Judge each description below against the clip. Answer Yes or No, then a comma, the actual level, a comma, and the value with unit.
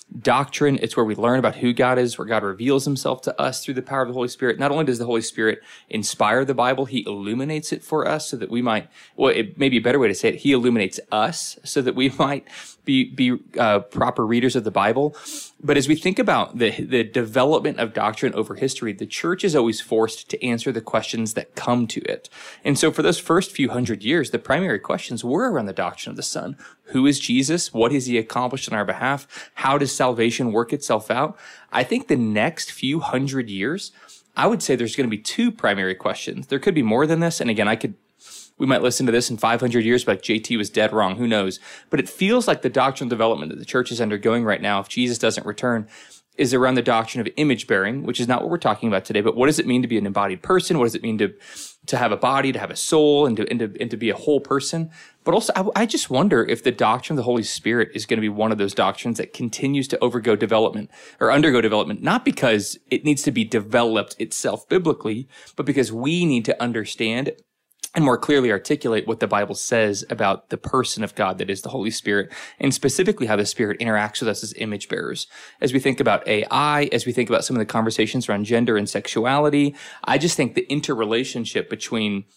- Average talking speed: No, fast, 240 wpm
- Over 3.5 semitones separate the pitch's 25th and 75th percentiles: Yes, average, 4.0 semitones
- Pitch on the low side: Yes, low, 125 Hz